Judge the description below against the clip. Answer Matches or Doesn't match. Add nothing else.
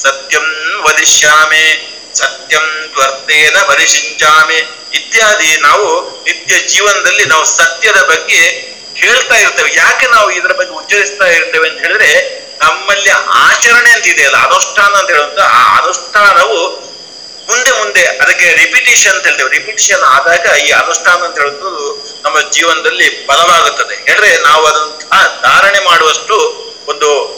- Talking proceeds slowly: Matches